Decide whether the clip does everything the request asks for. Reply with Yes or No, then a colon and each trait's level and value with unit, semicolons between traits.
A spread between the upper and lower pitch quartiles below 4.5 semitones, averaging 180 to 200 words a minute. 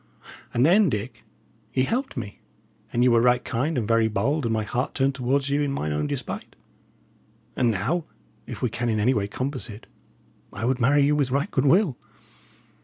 Yes: average, 3.7 semitones; average, 190 wpm